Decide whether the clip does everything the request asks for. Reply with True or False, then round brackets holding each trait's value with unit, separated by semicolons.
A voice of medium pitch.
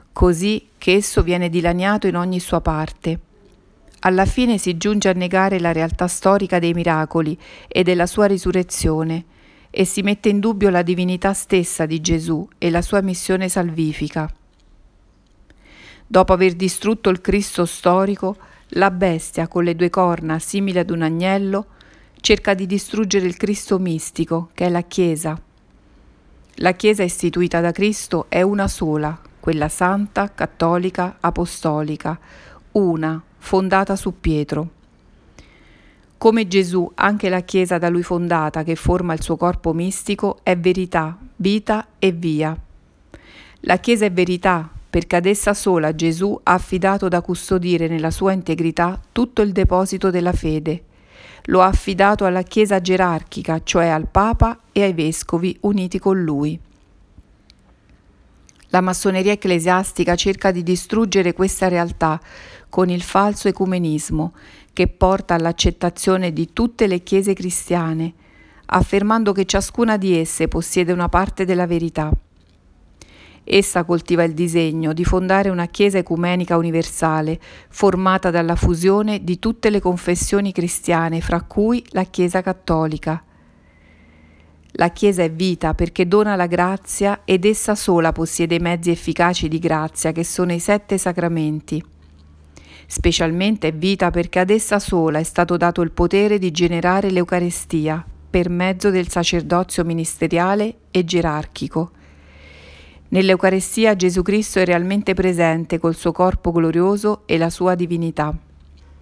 True (180 Hz)